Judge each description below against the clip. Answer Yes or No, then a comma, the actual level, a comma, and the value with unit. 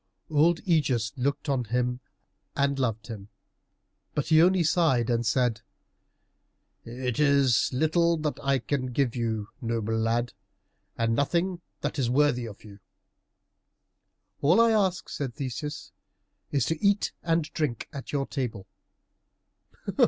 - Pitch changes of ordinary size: Yes, average, 4.7 semitones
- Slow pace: Yes, slow, 130 wpm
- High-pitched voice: No, low, 135 Hz